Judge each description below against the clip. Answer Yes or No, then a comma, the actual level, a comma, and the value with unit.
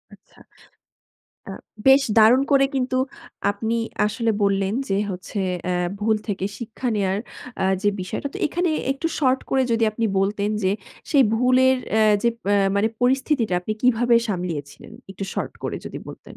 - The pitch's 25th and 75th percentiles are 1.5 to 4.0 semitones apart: No, average, 4.5 semitones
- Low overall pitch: No, high, 220 Hz